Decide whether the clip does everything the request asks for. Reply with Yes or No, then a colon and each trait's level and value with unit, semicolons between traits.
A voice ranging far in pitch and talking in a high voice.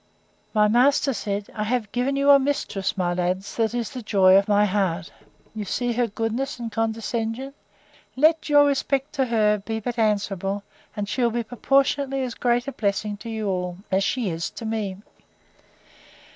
No: average, 3.8 semitones; high, 225 Hz